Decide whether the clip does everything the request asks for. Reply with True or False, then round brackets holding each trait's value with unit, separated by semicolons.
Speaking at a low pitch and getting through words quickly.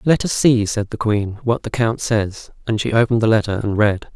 True (110 Hz; 245 wpm)